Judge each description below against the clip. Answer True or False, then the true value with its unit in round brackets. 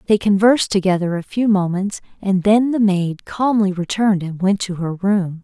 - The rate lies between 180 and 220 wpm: True (190 wpm)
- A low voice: False (195 Hz)